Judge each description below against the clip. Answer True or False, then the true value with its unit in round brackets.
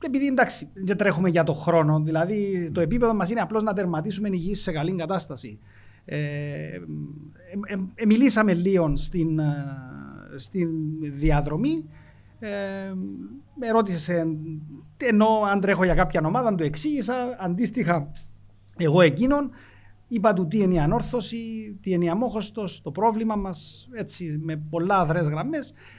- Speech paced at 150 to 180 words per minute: False (140 wpm)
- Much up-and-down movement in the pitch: True (5.8 semitones)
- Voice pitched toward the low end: False (180 Hz)